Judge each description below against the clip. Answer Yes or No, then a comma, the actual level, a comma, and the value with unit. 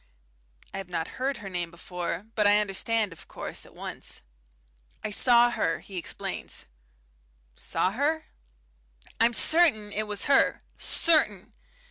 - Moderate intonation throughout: Yes, average, 4.0 semitones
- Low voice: No, high, 210 Hz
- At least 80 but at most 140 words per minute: Yes, slow, 135 wpm